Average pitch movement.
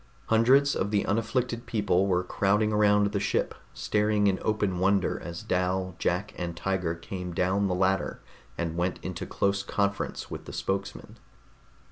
No: narrow, 2.3 semitones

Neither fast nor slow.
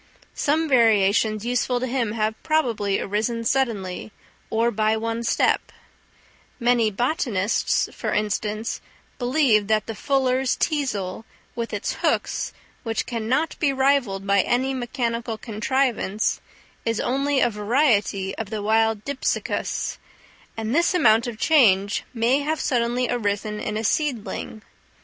No: slow, 130 wpm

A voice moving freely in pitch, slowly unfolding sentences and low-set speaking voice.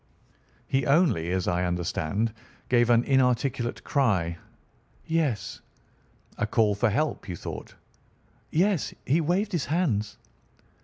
Yes: wide, 7.3 semitones; slow, 115 wpm; low, 120 Hz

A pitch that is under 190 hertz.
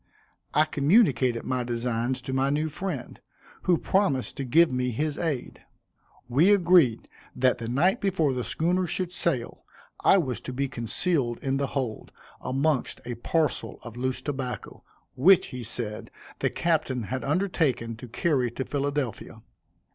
Yes: low, 135 Hz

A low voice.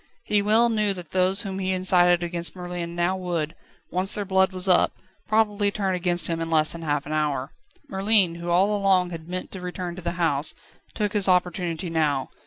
No: medium, 180 Hz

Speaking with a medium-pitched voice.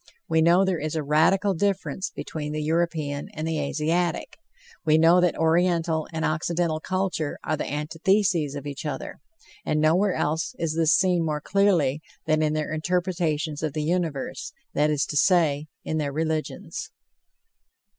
Yes: medium, 160 Hz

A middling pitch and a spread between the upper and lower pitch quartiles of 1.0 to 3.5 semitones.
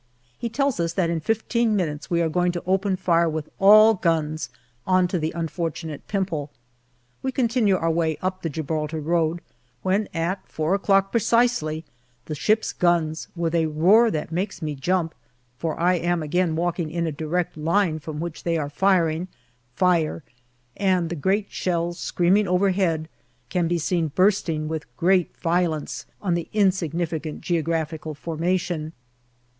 Yes: medium, 170 Hz; average, 2.9 semitones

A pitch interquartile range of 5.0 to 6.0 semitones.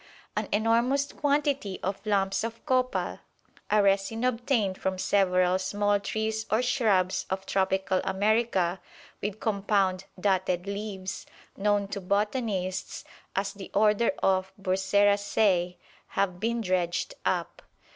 No: narrow, 2.5 semitones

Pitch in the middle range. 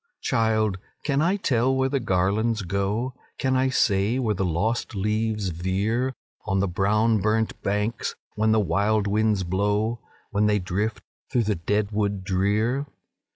No: low, 105 Hz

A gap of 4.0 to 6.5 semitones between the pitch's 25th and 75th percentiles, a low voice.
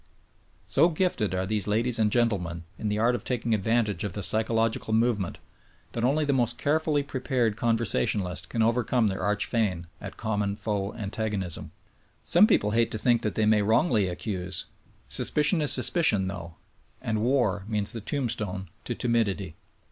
No: average, 3.1 semitones; low, 110 Hz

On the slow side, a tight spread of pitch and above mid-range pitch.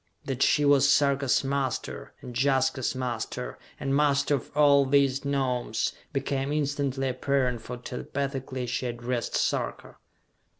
No: slow, 125 wpm; narrow, 1.8 semitones; low, 135 Hz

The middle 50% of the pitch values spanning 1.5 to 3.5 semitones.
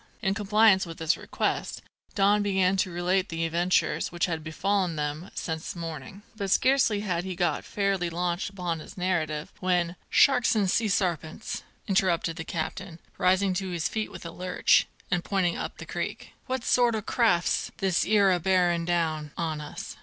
Yes: average, 2.8 semitones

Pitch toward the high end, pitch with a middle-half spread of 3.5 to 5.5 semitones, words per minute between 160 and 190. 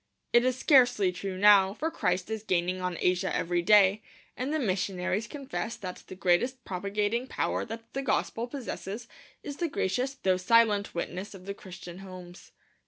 Yes: high, 200 Hz; average, 4.5 semitones; average, 170 wpm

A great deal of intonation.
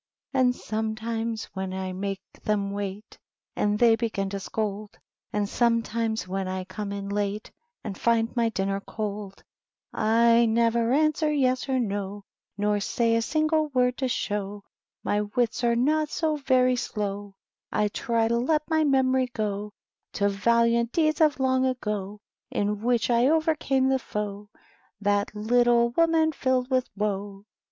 No: average, 3.8 semitones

